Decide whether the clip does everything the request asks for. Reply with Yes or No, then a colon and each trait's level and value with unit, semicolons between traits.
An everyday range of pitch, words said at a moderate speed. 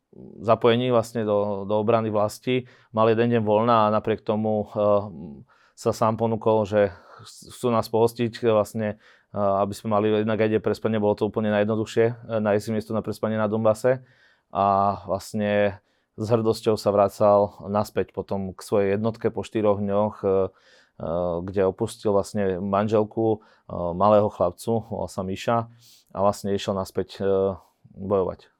No: narrow, 1.9 semitones; average, 155 wpm